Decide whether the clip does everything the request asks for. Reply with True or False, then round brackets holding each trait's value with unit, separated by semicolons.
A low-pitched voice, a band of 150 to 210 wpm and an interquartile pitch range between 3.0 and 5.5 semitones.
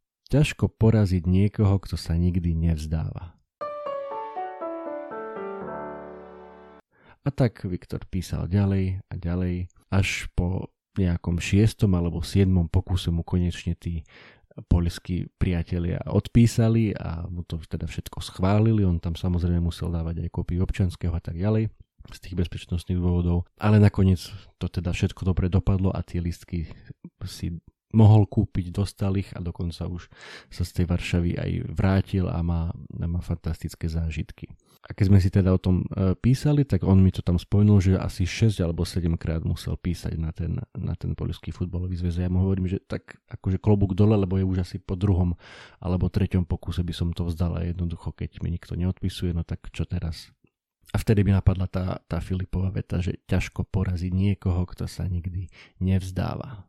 False (90 Hz; 160 wpm; 2.5 semitones)